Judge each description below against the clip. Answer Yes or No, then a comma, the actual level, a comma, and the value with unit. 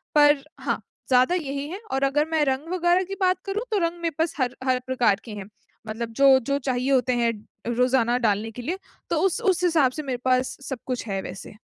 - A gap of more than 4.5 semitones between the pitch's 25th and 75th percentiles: Yes, average, 5.1 semitones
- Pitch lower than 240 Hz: No, very high, 270 Hz